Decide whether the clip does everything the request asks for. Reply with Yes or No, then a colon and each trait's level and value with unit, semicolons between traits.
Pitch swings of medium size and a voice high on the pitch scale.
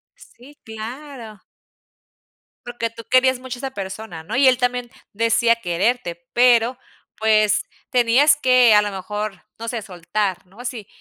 Yes: average, 3.1 semitones; high, 230 Hz